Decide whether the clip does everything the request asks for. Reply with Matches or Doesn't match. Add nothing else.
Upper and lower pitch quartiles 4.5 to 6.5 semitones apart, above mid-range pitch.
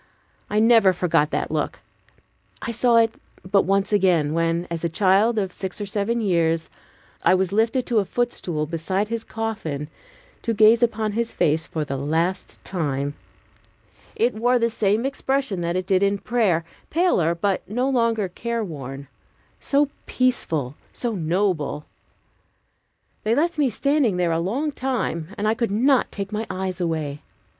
Matches